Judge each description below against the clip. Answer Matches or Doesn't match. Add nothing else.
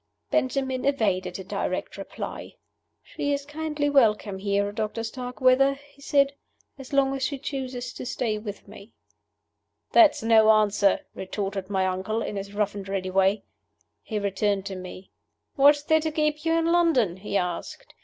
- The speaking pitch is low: Doesn't match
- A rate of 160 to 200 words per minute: Matches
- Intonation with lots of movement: Matches